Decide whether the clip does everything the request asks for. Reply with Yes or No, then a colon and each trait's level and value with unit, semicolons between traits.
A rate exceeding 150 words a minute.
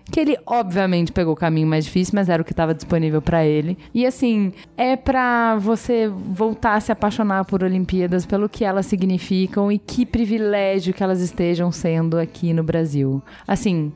Yes: average, 180 wpm